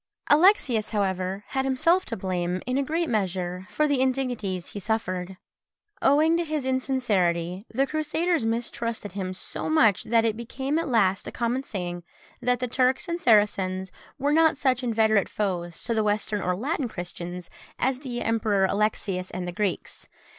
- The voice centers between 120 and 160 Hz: No, high, 225 Hz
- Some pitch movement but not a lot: No, wide, 5.9 semitones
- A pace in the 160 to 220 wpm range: Yes, average, 165 wpm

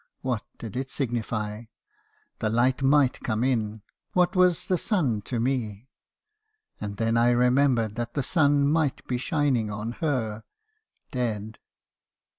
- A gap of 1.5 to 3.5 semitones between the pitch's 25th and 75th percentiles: No, average, 4.2 semitones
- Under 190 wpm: Yes, average, 140 wpm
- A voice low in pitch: Yes, low, 125 Hz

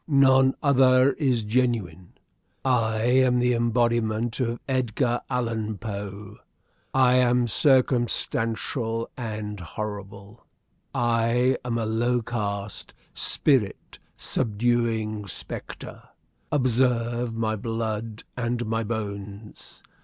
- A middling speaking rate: No, slow, 95 wpm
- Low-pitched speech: Yes, low, 115 Hz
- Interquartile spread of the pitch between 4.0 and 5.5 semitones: No, narrow, 2.4 semitones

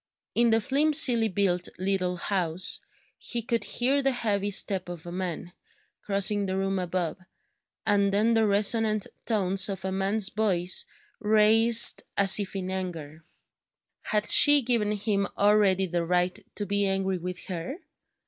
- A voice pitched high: Yes, high, 200 Hz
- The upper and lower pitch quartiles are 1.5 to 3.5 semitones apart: Yes, average, 2.8 semitones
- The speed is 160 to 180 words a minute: No, average, 150 wpm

